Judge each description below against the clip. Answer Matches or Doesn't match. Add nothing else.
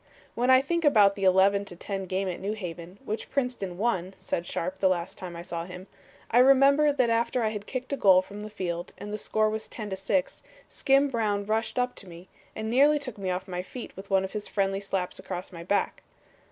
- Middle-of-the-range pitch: Doesn't match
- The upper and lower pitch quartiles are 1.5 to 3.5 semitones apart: Doesn't match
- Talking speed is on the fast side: Matches